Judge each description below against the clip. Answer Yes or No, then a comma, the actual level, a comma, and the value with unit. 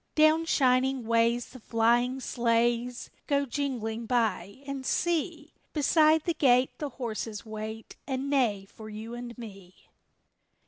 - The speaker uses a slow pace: Yes, slow, 130 wpm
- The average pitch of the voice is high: Yes, high, 245 Hz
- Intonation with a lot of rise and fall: No, average, 3.7 semitones